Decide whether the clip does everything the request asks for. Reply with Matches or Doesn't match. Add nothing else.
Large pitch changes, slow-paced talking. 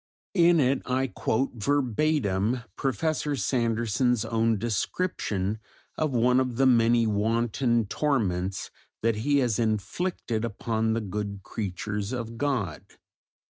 Doesn't match